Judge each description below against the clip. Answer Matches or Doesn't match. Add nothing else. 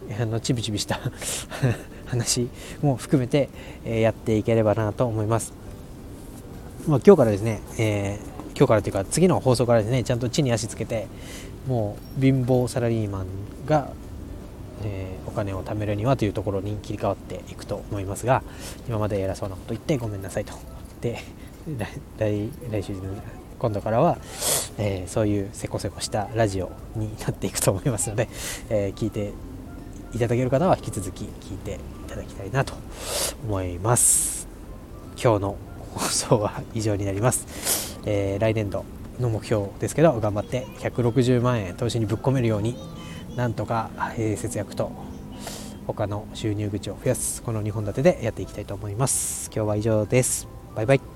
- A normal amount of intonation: Matches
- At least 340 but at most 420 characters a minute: Doesn't match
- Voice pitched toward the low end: Matches